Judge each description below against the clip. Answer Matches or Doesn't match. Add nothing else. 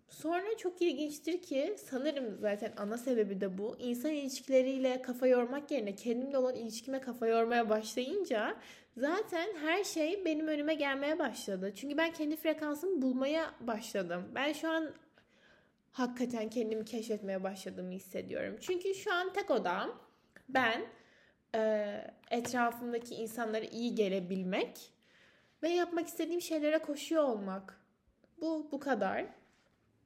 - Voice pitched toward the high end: Matches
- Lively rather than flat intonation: Matches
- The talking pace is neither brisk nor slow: Matches